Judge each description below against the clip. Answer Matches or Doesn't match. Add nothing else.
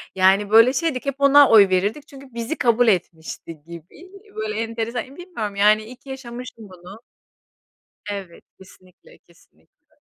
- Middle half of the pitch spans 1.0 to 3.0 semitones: Doesn't match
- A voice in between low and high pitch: Doesn't match